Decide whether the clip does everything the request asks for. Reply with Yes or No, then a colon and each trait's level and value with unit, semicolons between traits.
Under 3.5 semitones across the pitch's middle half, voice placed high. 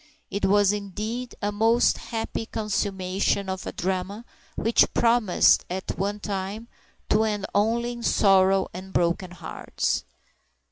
Yes: average, 2.7 semitones; high, 205 Hz